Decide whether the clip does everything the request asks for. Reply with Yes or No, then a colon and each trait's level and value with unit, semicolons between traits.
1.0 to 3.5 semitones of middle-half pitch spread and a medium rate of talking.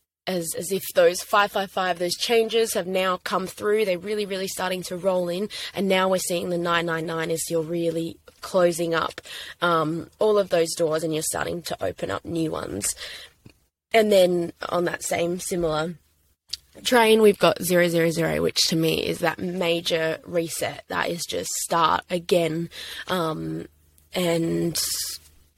Yes: narrow, 2.4 semitones; average, 170 wpm